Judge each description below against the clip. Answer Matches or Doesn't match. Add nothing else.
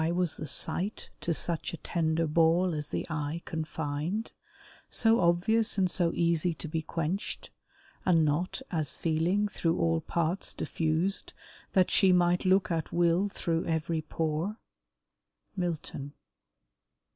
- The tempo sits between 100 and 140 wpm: Matches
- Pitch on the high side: Doesn't match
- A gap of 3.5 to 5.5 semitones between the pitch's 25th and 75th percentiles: Doesn't match